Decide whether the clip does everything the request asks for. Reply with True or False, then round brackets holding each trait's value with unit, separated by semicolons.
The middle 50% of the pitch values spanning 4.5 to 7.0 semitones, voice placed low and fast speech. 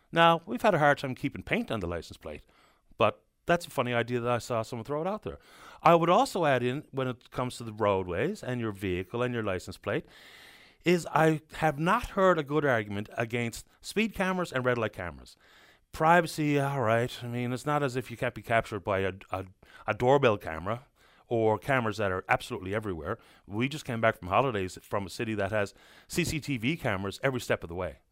True (5.5 semitones; 125 Hz; 215 wpm)